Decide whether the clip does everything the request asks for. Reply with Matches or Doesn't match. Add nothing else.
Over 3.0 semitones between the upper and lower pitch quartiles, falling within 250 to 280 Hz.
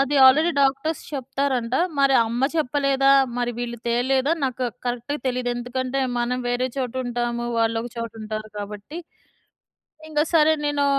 Doesn't match